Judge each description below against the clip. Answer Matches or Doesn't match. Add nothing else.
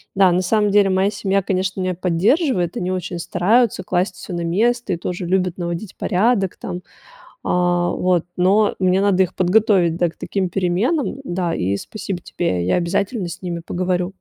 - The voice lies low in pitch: Doesn't match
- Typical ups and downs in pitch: Doesn't match